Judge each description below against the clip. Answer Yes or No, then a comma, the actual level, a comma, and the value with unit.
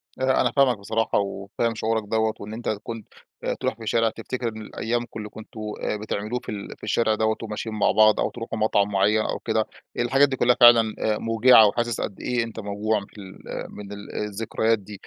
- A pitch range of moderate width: No, narrow, 1.8 semitones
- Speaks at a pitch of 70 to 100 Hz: No, low, 110 Hz